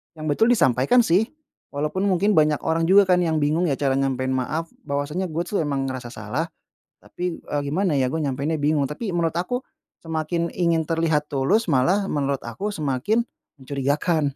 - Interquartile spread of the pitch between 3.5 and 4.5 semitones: Yes, average, 4.1 semitones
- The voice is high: No, medium, 155 Hz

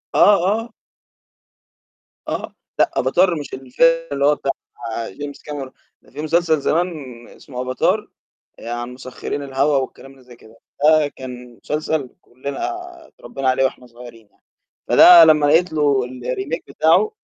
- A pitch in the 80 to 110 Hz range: No, medium, 140 Hz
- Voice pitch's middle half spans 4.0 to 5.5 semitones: No, average, 3.5 semitones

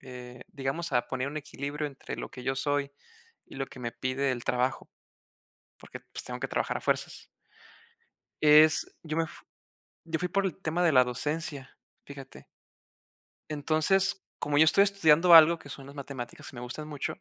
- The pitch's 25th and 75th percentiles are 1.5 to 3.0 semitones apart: No, average, 3.4 semitones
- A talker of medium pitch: Yes, medium, 145 Hz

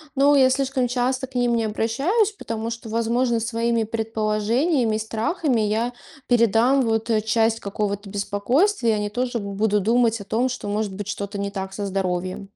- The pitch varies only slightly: No, average, 3.0 semitones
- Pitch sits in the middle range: No, high, 225 Hz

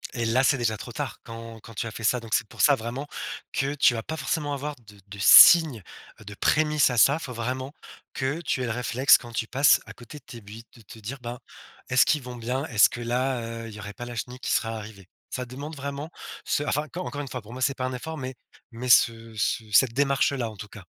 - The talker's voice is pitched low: Yes, low, 125 Hz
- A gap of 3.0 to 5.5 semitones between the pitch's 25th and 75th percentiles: Yes, average, 3.3 semitones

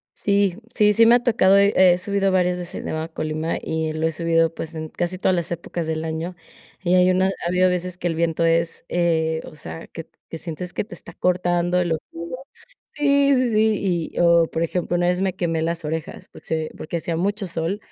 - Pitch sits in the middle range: Yes, medium, 175 Hz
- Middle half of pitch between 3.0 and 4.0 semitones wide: No, narrow, 2.4 semitones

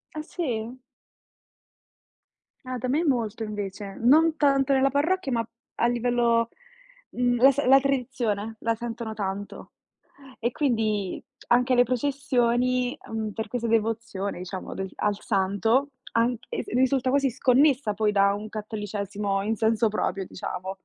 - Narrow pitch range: No, average, 3.5 semitones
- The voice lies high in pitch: Yes, high, 230 Hz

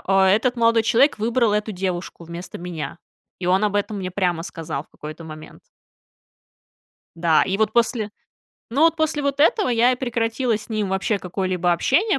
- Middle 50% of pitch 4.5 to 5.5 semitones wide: Yes, average, 5.0 semitones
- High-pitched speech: Yes, high, 210 Hz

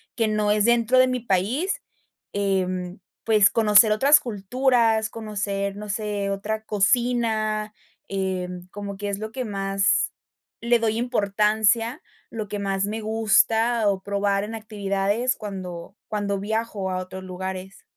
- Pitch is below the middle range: No, high, 210 Hz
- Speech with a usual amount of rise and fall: No, narrow, 2.3 semitones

